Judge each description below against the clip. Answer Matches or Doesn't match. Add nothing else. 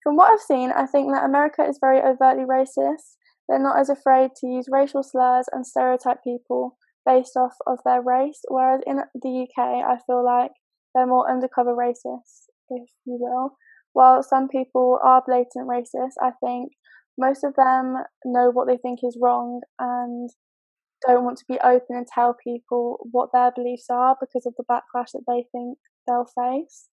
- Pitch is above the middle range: Matches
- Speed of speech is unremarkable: Matches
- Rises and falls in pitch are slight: Matches